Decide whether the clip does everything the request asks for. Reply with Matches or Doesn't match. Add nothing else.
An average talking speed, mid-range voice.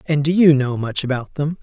Doesn't match